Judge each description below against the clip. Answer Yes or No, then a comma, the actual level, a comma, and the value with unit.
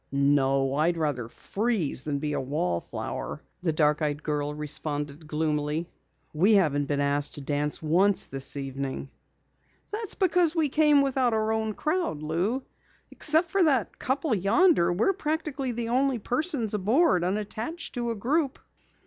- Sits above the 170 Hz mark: Yes, medium, 185 Hz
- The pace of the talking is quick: No, average, 150 wpm